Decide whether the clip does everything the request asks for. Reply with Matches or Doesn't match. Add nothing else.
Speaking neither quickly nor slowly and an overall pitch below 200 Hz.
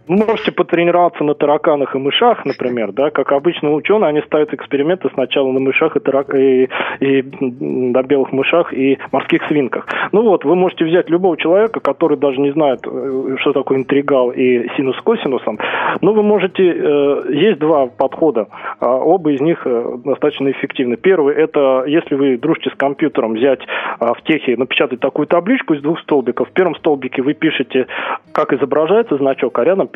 Doesn't match